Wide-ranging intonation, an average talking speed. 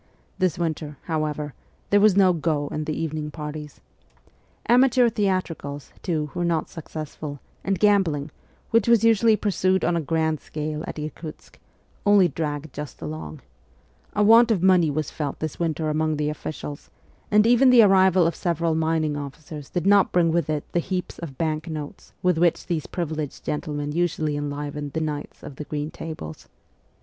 No: average, 3.6 semitones; average, 170 wpm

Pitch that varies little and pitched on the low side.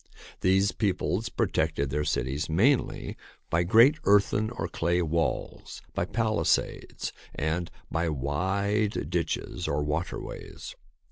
No: average, 5.0 semitones; very low, 90 Hz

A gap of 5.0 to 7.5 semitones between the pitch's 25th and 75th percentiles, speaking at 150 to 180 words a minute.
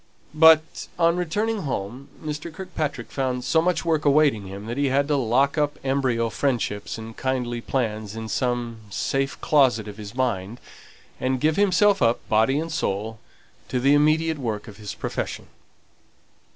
Yes: average, 5.3 semitones; average, 160 wpm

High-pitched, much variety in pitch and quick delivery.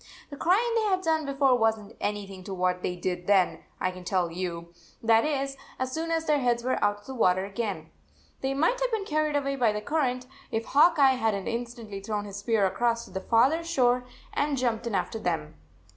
Yes: high, 235 Hz; wide, 6.1 semitones; fast, 225 wpm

